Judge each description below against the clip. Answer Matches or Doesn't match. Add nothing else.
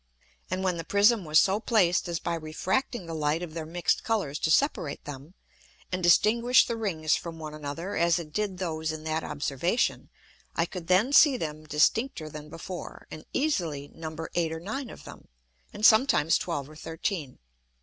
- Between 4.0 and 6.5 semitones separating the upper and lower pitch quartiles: Matches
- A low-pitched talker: Doesn't match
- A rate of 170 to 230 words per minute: Matches